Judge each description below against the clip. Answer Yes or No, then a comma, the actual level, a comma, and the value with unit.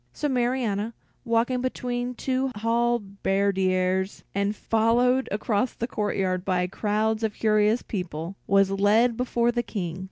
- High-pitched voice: Yes, high, 215 Hz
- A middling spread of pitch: Yes, average, 3.5 semitones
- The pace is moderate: No, slow, 125 wpm